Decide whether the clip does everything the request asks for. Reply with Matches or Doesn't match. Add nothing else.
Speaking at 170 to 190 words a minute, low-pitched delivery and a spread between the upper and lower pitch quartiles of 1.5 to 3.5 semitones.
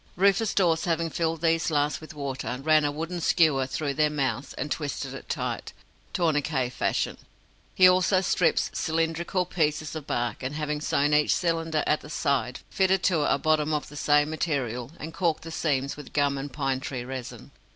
Doesn't match